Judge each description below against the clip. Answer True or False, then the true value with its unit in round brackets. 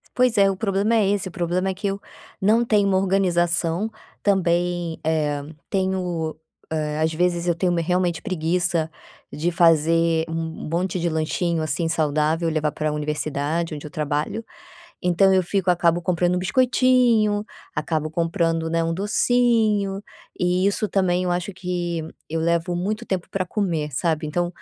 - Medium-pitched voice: True (175 Hz)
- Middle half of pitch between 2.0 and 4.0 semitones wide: True (3.0 semitones)